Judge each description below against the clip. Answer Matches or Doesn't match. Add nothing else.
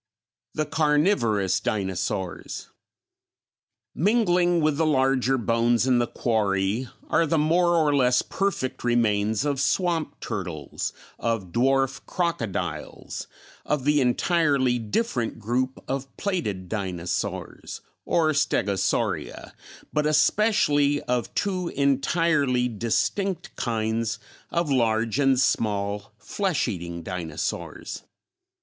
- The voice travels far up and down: Matches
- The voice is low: Matches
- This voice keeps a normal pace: Doesn't match